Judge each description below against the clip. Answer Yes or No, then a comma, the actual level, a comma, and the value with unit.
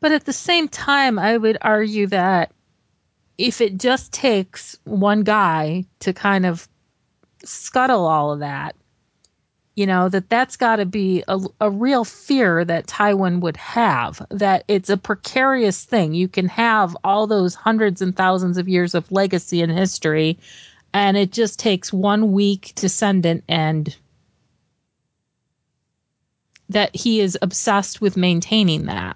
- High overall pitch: Yes, high, 195 Hz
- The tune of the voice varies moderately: Yes, average, 3.1 semitones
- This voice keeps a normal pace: Yes, average, 145 wpm